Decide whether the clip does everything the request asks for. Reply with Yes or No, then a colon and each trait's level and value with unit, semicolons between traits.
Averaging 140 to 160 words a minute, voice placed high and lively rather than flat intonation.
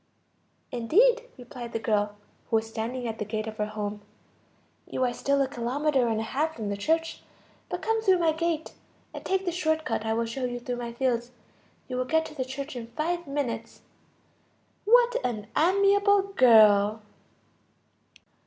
No: average, 175 wpm; very high, 255 Hz; wide, 6.2 semitones